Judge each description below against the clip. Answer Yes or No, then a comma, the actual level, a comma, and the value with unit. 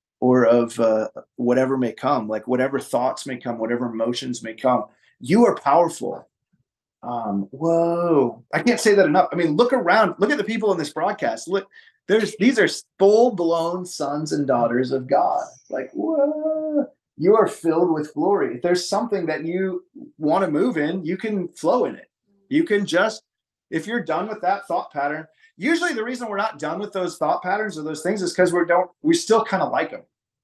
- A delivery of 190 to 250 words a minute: Yes, average, 195 wpm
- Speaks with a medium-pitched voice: Yes, medium, 175 Hz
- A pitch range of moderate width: No, wide, 7.5 semitones